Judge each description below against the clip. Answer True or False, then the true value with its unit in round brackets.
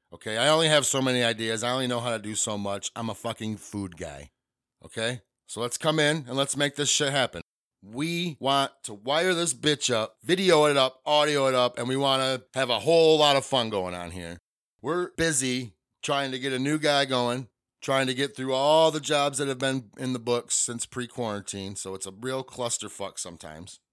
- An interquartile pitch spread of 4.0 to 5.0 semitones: True (4.3 semitones)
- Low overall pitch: True (130 Hz)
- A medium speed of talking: False (220 wpm)